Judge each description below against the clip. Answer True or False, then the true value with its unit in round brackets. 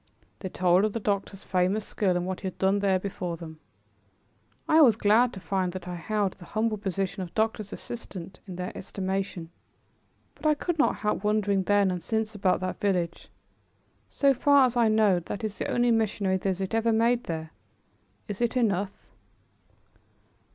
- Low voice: False (200 Hz)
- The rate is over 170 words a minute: True (180 wpm)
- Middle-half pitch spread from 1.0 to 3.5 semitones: True (3.1 semitones)